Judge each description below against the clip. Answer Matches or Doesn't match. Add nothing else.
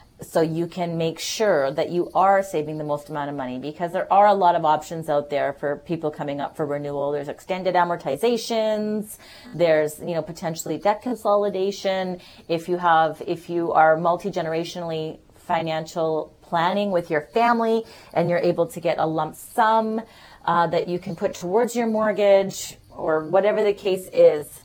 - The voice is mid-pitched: Matches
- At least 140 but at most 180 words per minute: Matches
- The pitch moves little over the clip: Doesn't match